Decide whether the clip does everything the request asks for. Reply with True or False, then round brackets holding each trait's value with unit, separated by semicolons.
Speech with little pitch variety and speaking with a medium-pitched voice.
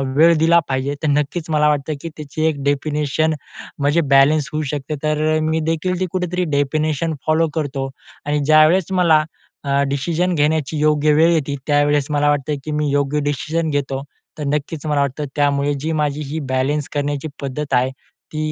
True (1.7 semitones; 150 Hz)